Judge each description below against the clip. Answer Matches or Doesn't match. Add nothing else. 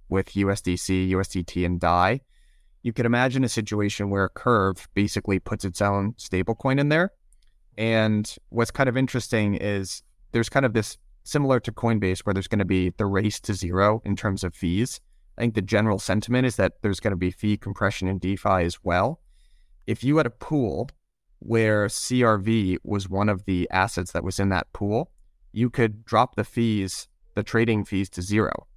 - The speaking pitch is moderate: Doesn't match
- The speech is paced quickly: Doesn't match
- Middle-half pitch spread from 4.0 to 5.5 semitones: Doesn't match